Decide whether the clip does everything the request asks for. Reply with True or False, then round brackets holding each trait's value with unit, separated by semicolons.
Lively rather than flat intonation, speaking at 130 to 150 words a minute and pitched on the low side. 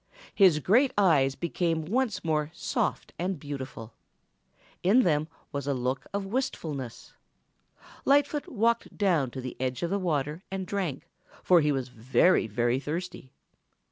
False (6.3 semitones; 140 wpm; 160 Hz)